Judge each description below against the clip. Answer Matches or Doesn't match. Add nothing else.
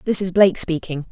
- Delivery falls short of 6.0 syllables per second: Doesn't match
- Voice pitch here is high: Doesn't match